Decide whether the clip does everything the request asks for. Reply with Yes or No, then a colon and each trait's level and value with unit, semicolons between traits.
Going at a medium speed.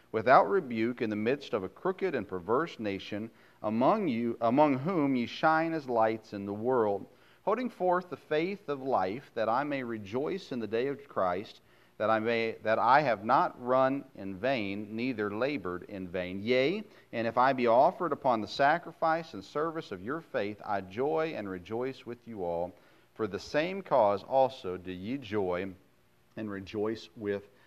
Yes: average, 180 wpm